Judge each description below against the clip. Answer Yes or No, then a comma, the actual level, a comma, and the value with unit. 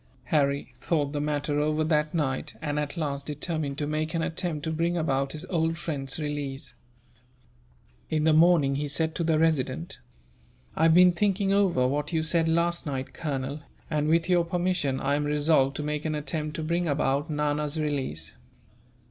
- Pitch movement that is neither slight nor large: No, narrow, 2.3 semitones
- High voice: No, medium, 150 Hz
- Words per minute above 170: Yes, average, 180 wpm